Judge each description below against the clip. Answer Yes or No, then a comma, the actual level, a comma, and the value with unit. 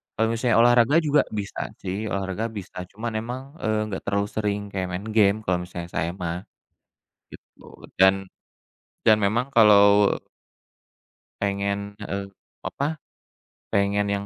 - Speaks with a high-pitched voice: No, low, 100 Hz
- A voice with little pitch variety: Yes, narrow, 2.2 semitones